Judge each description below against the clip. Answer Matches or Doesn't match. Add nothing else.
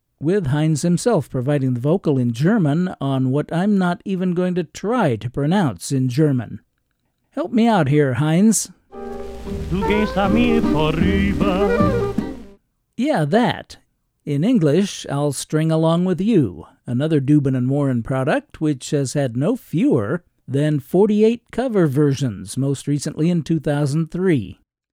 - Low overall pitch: Doesn't match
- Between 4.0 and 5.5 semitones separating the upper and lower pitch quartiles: Matches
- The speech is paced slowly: Matches